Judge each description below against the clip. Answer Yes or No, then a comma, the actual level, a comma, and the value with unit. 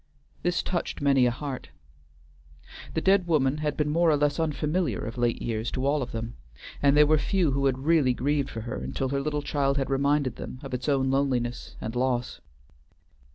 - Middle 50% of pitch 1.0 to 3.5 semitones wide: Yes, average, 2.7 semitones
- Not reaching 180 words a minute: No, average, 200 wpm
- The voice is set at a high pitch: No, medium, 140 Hz